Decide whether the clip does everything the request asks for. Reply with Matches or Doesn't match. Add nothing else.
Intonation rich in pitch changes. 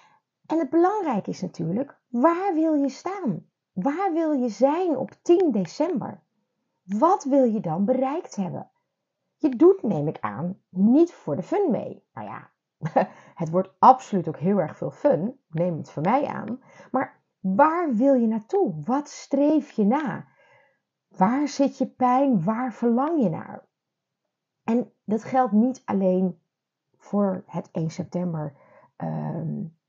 Matches